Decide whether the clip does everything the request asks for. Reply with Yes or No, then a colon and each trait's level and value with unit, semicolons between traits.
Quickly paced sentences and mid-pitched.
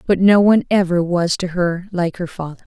Yes: fast, 220 wpm; medium, 180 Hz